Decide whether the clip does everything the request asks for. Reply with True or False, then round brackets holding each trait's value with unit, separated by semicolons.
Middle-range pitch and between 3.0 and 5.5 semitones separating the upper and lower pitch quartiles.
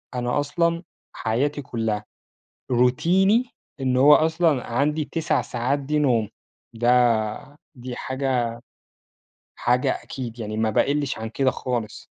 False (130 Hz; 3.7 semitones)